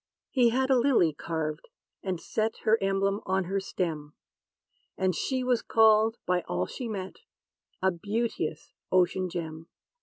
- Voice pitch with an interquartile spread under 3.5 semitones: No, average, 4.7 semitones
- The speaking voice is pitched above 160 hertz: Yes, high, 190 Hz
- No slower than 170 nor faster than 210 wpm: No, average, 145 wpm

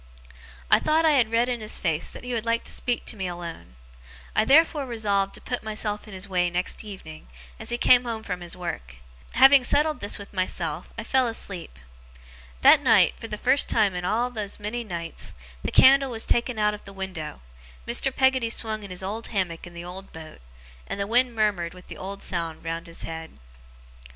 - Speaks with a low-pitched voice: No, high, 210 Hz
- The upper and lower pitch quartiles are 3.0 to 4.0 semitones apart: No, average, 5.0 semitones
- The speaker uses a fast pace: Yes, fast, 210 wpm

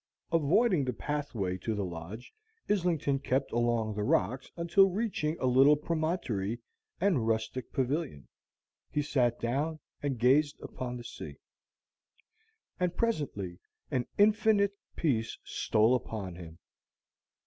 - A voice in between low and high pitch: No, low, 130 Hz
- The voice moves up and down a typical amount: No, wide, 6.3 semitones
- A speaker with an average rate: No, slow, 120 wpm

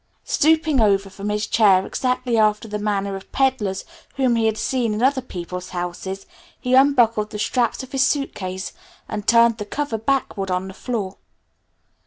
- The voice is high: Yes, high, 215 Hz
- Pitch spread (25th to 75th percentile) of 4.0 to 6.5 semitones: Yes, average, 4.5 semitones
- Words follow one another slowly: No, average, 170 wpm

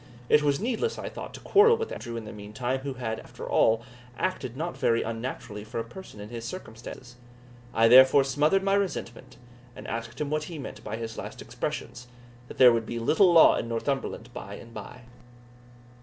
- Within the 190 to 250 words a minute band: Yes, average, 195 wpm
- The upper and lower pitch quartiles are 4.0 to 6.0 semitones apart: Yes, average, 4.9 semitones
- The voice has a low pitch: Yes, low, 125 Hz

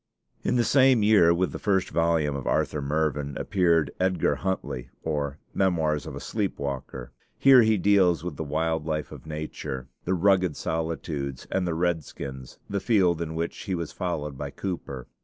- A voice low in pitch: Yes, very low, 80 Hz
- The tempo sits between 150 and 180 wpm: Yes, average, 175 wpm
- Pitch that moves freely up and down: No, average, 4.1 semitones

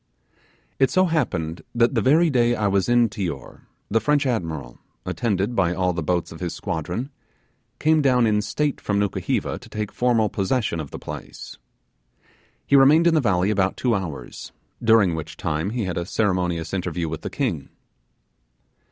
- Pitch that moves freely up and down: Yes, wide, 5.9 semitones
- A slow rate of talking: No, average, 170 wpm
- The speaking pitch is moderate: No, low, 100 Hz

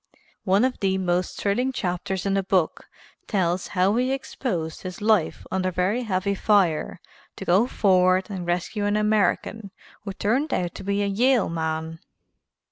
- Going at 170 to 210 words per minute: No, average, 160 wpm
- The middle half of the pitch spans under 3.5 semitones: Yes, average, 2.7 semitones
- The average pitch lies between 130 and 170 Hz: No, high, 195 Hz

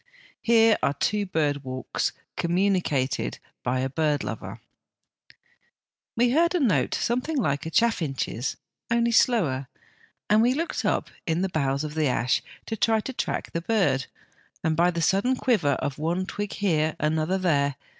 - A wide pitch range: Yes, wide, 7.7 semitones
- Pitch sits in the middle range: Yes, medium, 170 Hz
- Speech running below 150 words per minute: No, average, 155 wpm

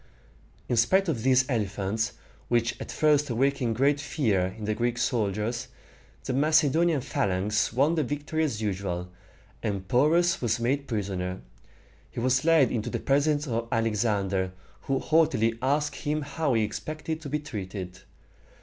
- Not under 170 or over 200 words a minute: No, average, 150 wpm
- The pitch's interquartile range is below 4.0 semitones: No, wide, 5.6 semitones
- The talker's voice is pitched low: Yes, low, 120 Hz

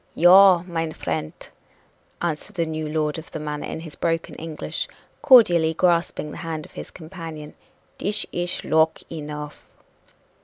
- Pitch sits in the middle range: Yes, medium, 160 Hz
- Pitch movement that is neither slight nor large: No, narrow, 2.2 semitones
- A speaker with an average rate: Yes, average, 145 wpm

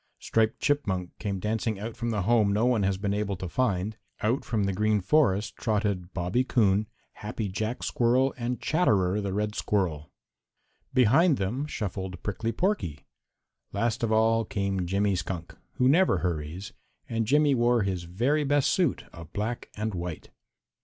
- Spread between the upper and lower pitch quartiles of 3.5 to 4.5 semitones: Yes, average, 4.0 semitones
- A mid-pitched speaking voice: No, low, 105 Hz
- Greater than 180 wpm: No, average, 160 wpm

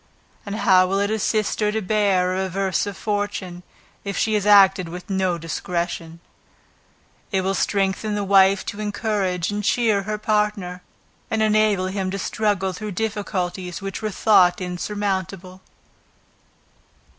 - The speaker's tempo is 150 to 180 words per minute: No, average, 140 wpm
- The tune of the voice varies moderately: No, narrow, 2.2 semitones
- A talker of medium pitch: No, high, 195 Hz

